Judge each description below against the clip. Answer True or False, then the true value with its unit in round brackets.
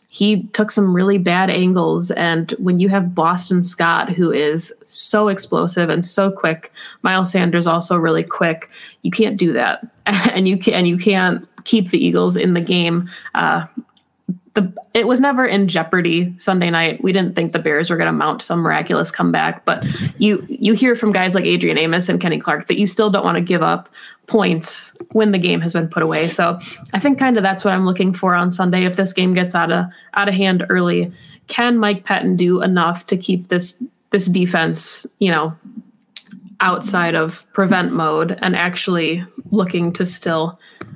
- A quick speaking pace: False (195 wpm)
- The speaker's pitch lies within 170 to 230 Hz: True (185 Hz)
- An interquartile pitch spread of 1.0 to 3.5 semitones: True (3.2 semitones)